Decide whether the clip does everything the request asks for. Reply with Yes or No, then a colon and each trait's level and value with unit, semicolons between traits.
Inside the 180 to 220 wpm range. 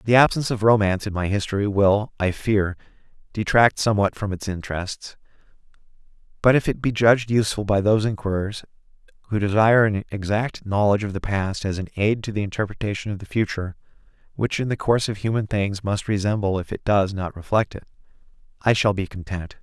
Yes: average, 185 wpm